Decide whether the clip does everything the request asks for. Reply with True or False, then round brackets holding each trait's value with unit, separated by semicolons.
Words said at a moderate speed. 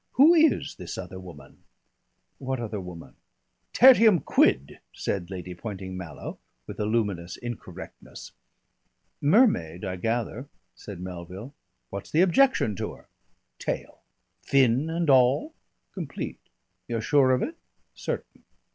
False (120 wpm)